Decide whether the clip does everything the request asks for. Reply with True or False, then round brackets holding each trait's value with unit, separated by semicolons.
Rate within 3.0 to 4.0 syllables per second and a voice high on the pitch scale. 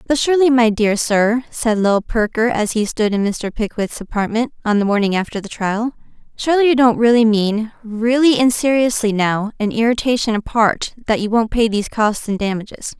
False (5.3 syllables/s; 225 Hz)